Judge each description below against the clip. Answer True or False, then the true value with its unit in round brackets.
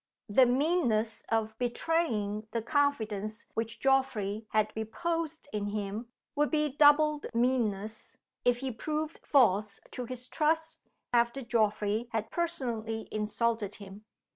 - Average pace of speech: False (120 wpm)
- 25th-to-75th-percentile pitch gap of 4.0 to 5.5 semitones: True (5.1 semitones)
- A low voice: False (235 Hz)